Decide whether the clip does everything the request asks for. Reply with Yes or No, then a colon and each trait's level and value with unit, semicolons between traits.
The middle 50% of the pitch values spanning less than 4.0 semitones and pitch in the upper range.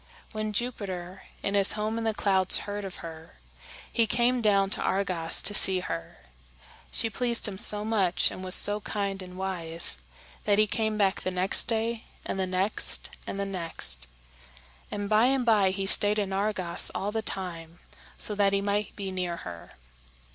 Yes: narrow, 2.4 semitones; high, 200 Hz